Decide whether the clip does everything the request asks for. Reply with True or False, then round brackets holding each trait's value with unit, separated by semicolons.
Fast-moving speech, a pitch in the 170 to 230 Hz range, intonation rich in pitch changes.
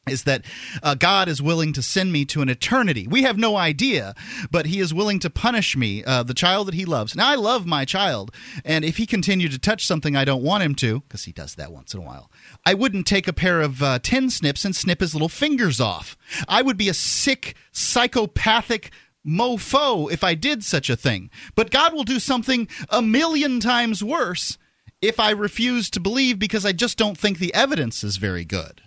True (220 wpm; 185 Hz; 7.9 semitones)